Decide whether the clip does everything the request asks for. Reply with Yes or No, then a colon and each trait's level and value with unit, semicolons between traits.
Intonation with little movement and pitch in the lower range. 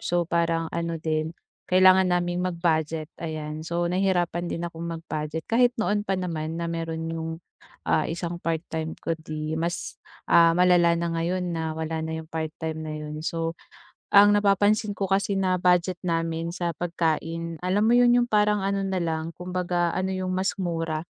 No: narrow, 2.2 semitones; medium, 170 Hz